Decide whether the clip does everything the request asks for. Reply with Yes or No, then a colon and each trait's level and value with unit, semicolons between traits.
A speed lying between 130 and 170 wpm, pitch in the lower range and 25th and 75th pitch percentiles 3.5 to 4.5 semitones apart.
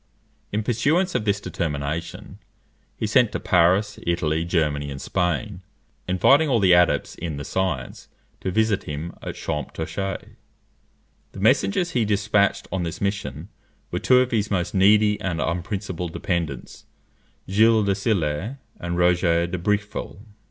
Yes: average, 140 wpm; very low, 95 Hz; average, 3.8 semitones